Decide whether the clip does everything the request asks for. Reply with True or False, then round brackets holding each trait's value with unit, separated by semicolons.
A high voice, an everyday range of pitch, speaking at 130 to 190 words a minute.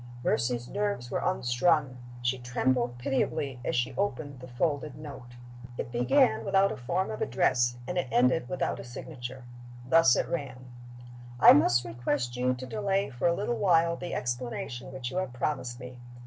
False (130 Hz; 4.7 semitones; 170 wpm)